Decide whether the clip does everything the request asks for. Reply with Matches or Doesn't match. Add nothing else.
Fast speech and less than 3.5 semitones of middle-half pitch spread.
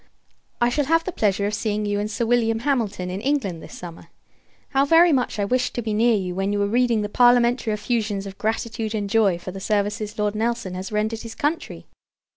Matches